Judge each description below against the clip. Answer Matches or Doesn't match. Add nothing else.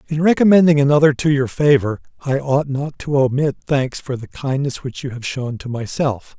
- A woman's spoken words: Doesn't match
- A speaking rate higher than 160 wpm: Matches